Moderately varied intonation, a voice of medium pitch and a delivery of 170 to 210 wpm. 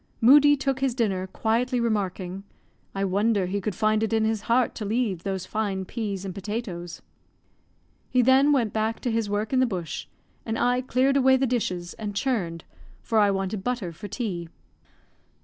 No: average, 4.3 semitones; high, 220 Hz; average, 180 wpm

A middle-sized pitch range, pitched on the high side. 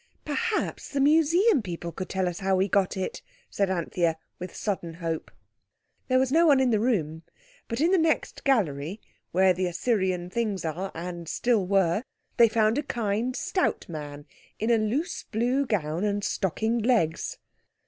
No: wide, 5.9 semitones; high, 205 Hz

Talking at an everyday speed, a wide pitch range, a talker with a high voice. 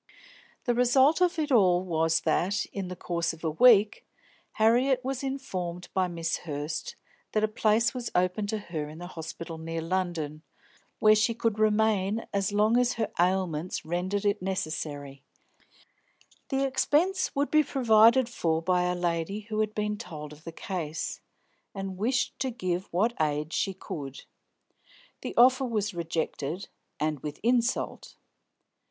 Yes: average, 155 wpm; wide, 5.7 semitones; high, 195 Hz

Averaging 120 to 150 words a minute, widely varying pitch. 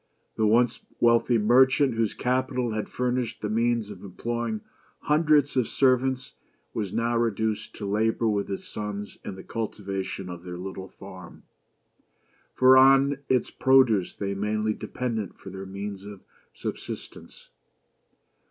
No: slow, 135 wpm; average, 4.0 semitones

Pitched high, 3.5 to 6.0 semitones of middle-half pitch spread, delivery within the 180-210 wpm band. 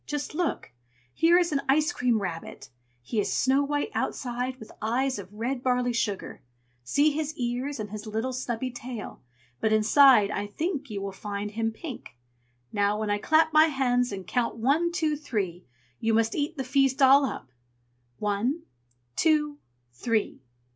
No: very high, 250 Hz; average, 5.2 semitones; average, 165 wpm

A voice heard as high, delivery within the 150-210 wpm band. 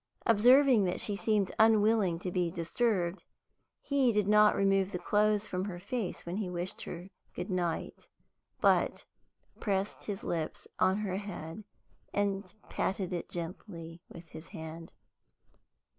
No: high, 195 Hz; slow, 135 wpm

